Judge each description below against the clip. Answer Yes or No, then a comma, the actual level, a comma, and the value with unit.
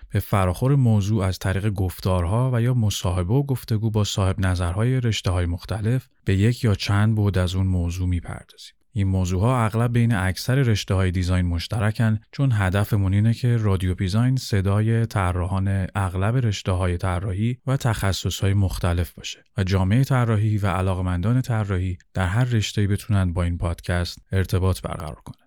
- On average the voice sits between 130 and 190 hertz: No, low, 100 Hz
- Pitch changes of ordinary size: Yes, average, 3.5 semitones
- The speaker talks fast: Yes, fast, 165 wpm